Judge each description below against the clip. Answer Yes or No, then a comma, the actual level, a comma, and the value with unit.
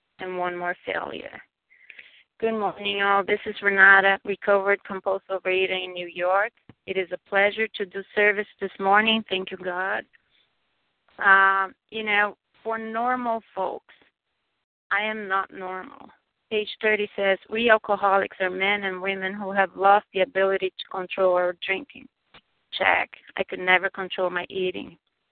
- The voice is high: Yes, high, 195 Hz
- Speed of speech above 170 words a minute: No, average, 150 wpm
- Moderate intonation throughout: No, narrow, 1.6 semitones